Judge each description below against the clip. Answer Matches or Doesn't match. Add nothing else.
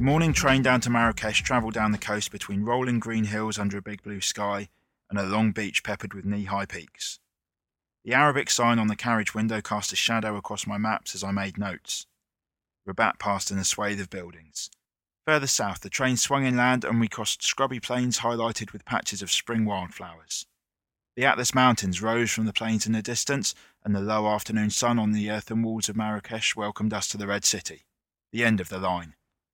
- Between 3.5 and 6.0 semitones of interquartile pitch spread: Doesn't match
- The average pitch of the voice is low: Matches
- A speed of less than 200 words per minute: Doesn't match